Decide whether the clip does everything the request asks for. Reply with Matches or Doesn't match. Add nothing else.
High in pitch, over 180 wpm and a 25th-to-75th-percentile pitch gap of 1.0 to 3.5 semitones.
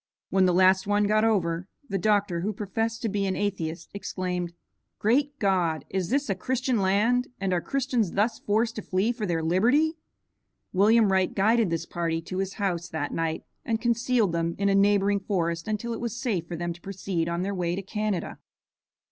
Doesn't match